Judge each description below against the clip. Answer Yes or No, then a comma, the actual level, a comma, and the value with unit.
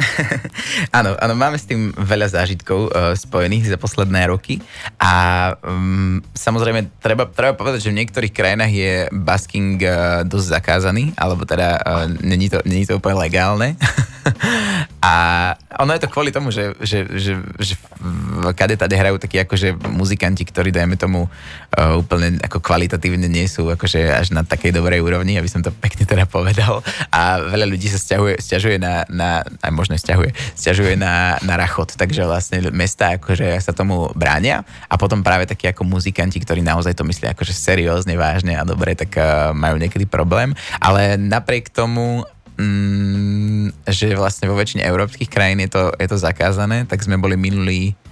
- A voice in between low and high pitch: No, very low, 95 Hz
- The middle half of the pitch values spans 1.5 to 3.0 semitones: Yes, narrow, 2.5 semitones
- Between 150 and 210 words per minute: Yes, average, 160 wpm